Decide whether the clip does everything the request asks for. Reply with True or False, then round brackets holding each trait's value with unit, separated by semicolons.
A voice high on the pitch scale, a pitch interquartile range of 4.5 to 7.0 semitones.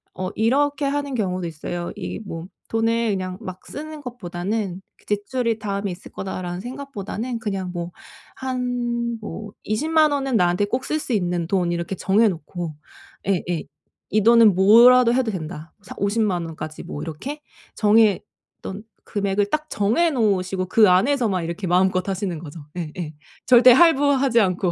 True (205 Hz; 5.2 semitones)